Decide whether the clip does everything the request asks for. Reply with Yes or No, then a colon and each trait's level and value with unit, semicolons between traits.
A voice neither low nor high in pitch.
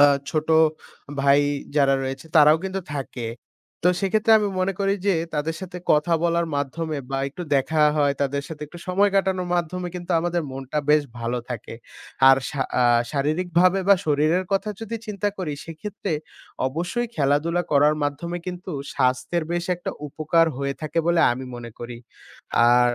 Yes: medium, 160 Hz